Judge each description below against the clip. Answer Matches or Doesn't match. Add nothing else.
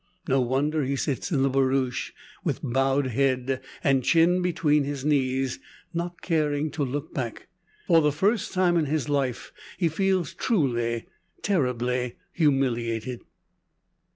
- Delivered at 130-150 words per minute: Matches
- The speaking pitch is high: Doesn't match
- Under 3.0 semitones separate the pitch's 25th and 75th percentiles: Doesn't match